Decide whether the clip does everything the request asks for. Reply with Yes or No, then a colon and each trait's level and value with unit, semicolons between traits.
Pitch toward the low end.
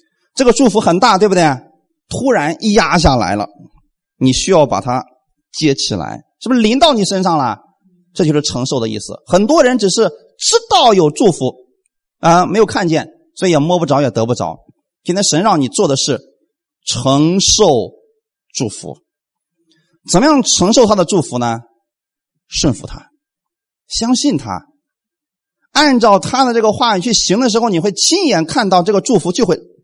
No: medium, 185 Hz